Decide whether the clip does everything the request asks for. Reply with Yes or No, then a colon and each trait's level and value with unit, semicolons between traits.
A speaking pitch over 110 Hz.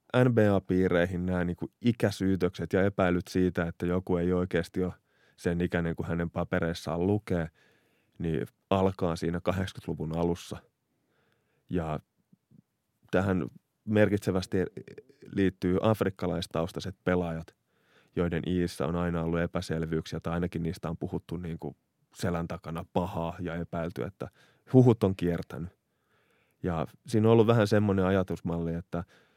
No: very low, 90 Hz